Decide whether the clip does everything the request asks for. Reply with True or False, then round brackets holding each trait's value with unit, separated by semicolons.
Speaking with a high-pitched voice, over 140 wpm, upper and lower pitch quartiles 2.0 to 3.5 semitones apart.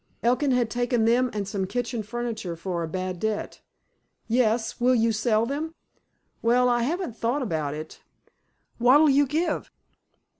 True (235 Hz; 150 wpm; 2.9 semitones)